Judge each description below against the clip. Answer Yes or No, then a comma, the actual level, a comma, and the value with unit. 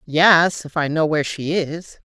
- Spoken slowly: No, average, 200 wpm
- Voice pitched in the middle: Yes, medium, 160 Hz